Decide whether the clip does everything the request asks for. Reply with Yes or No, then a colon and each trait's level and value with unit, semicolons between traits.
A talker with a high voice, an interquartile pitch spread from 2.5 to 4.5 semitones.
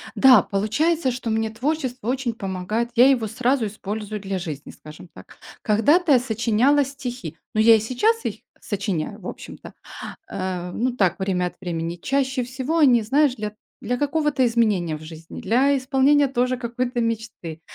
No: high, 230 Hz; average, 4.9 semitones